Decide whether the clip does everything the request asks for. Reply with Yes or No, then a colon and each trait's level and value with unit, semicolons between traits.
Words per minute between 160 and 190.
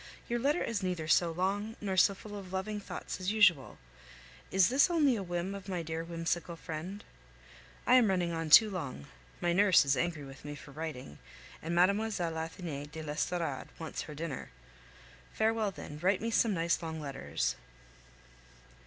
Yes: average, 170 wpm